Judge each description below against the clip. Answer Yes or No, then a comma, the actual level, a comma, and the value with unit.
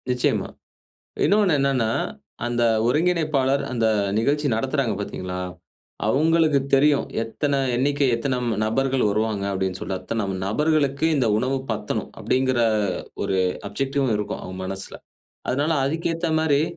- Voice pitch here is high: No, low, 135 Hz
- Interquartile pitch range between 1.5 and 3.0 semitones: No, average, 4.8 semitones